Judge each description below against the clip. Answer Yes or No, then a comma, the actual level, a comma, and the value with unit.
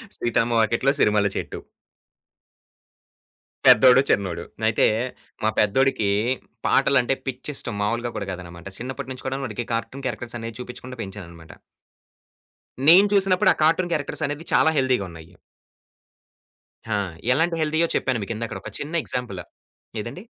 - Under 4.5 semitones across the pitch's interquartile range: No, average, 4.8 semitones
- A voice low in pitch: Yes, low, 120 Hz